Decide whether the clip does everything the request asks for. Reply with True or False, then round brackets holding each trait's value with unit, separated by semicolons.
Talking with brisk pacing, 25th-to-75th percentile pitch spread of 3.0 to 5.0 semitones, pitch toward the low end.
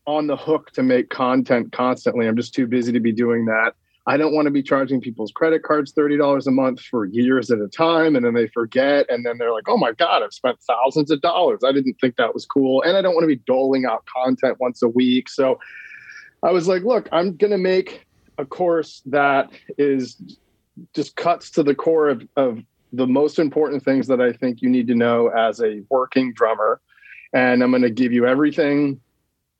True (220 wpm; 3.4 semitones; 130 Hz)